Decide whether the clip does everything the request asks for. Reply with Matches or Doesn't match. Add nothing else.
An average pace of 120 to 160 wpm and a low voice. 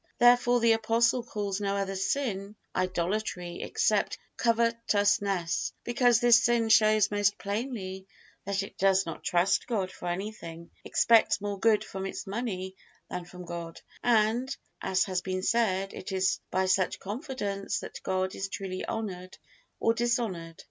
Doesn't match